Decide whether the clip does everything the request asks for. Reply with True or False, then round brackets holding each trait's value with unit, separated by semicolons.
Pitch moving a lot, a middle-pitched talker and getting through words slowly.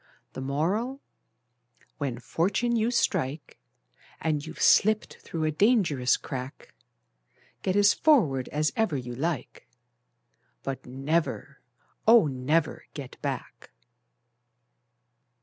True (7.2 semitones; 155 Hz; 100 wpm)